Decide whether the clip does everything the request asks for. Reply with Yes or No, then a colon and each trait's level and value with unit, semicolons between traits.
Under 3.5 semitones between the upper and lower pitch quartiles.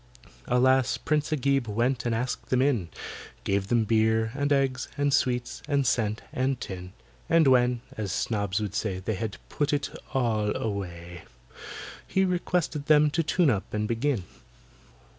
No: average, 4.9 semitones